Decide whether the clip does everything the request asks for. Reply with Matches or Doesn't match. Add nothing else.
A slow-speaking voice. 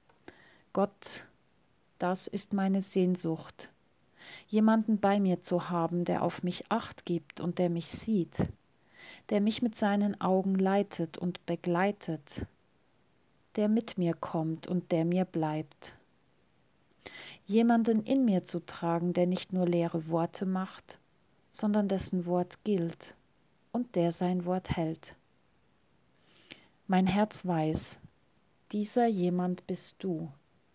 Matches